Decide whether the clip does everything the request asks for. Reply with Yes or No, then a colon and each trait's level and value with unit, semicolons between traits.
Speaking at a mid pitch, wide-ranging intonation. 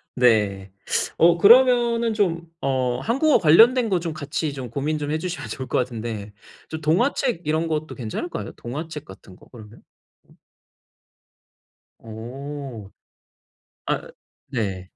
Yes: medium, 150 Hz; wide, 6.6 semitones